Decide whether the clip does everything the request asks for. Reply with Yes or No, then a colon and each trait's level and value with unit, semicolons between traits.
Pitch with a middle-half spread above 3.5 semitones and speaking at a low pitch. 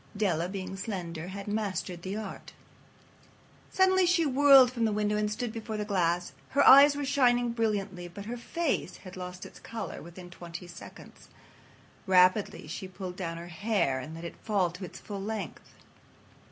No: average, 4.3 semitones; high, 200 Hz